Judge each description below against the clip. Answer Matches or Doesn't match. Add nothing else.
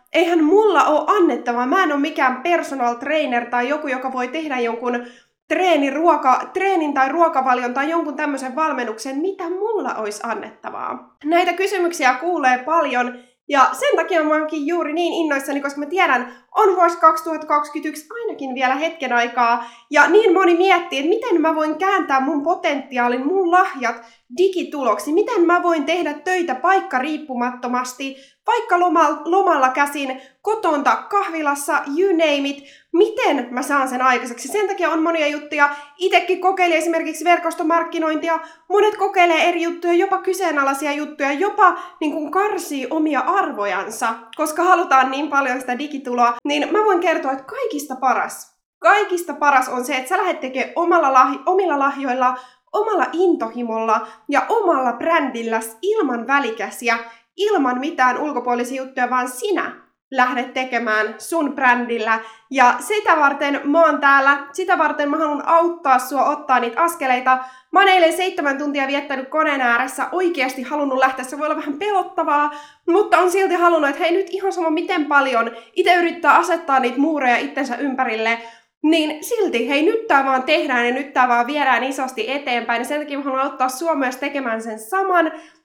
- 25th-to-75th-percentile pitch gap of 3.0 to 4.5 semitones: Doesn't match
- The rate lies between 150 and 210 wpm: Matches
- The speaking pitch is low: Doesn't match